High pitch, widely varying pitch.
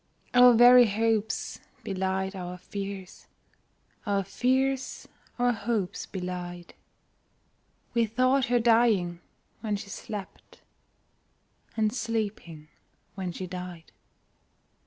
No: high, 205 Hz; average, 4.3 semitones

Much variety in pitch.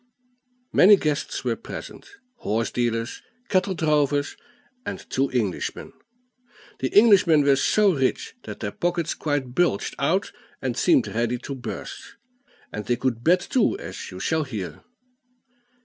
Yes: wide, 6.4 semitones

